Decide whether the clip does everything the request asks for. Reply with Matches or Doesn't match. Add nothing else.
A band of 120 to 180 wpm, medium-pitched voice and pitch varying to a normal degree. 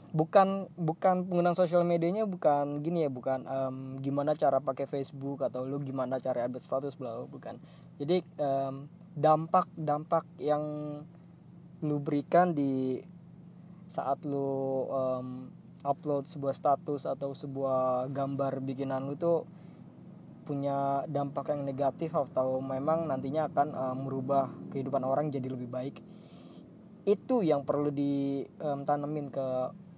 Matches